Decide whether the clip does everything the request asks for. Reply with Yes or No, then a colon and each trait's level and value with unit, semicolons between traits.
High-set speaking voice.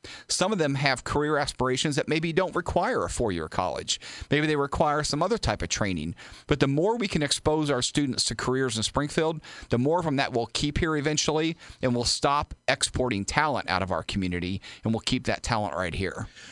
No: medium, 140 Hz